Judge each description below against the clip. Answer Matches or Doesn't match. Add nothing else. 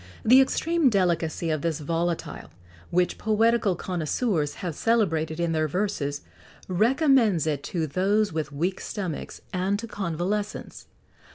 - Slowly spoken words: Matches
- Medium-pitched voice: Matches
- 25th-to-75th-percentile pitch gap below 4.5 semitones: Doesn't match